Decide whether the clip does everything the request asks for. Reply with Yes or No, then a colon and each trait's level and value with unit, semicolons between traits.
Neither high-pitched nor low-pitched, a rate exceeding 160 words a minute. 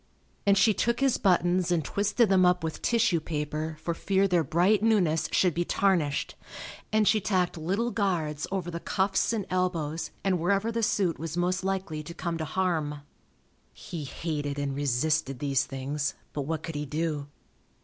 Yes: medium, 170 Hz; average, 175 wpm